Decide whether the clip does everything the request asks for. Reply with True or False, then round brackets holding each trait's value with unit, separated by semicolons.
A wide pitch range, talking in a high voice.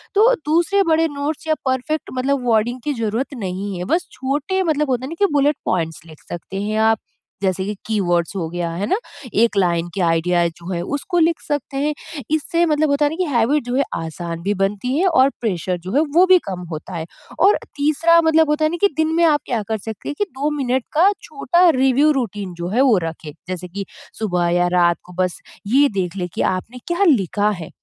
True (8.7 semitones; 245 Hz)